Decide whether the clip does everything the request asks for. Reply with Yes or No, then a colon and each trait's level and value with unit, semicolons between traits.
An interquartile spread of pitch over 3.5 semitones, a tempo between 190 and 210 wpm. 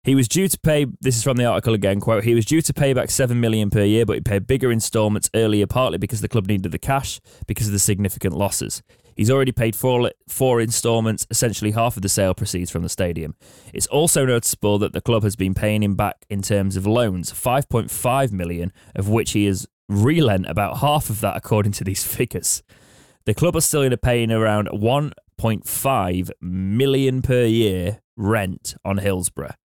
Yes: average, 3.9 semitones; average, 195 wpm